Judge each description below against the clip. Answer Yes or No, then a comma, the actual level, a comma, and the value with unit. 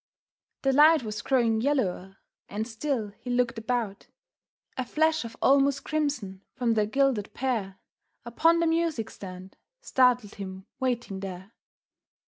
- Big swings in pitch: No, average, 4.9 semitones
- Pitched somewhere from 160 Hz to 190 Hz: No, high, 240 Hz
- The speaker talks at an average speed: No, slow, 130 wpm